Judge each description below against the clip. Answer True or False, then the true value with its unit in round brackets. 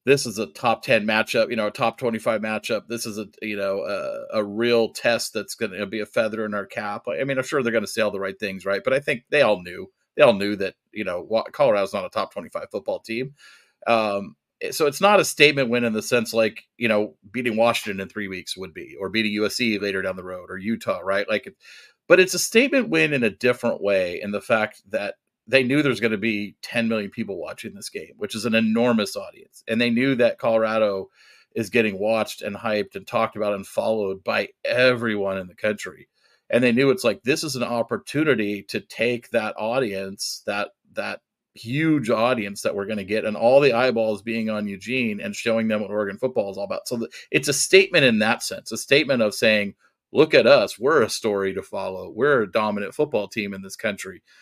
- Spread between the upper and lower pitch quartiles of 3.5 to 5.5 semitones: False (3.1 semitones)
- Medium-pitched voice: False (110 Hz)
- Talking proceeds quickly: True (230 wpm)